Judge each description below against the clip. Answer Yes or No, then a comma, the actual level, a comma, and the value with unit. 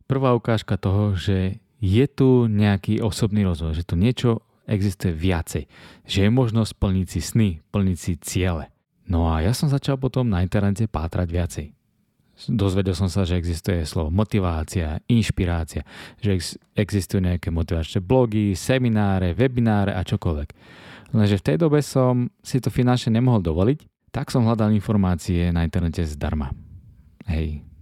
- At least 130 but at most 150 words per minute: Yes, average, 145 wpm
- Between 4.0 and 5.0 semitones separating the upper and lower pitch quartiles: Yes, average, 4.6 semitones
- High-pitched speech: No, low, 100 Hz